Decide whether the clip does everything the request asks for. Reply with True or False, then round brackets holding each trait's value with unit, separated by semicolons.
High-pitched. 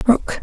True (240 Hz)